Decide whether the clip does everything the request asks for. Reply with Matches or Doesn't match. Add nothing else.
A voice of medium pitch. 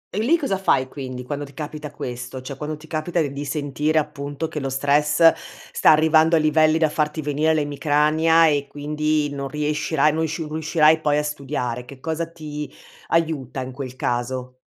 Matches